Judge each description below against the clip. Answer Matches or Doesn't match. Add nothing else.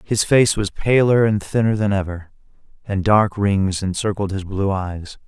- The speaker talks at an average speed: Matches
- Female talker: Doesn't match